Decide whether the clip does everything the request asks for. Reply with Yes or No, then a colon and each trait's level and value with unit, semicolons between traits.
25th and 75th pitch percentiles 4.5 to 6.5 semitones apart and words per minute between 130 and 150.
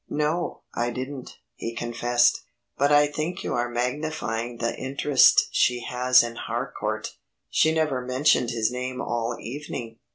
No: average, 3.4 semitones; average, 140 wpm